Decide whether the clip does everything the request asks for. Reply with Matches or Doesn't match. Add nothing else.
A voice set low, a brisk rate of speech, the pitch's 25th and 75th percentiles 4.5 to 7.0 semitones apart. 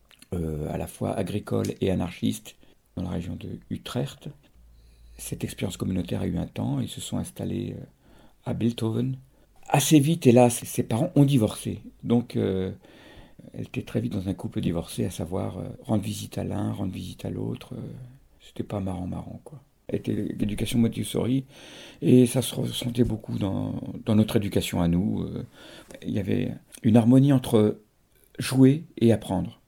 Doesn't match